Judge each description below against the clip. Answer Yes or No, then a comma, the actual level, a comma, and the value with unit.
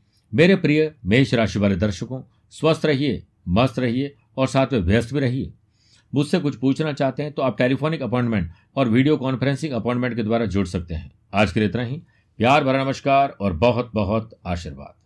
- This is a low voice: Yes, low, 125 Hz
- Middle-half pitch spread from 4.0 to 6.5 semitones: Yes, average, 4.5 semitones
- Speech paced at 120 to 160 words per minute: No, average, 185 wpm